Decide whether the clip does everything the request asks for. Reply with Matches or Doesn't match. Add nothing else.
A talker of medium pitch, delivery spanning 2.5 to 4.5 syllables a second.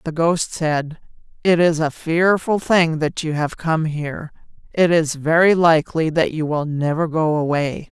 Matches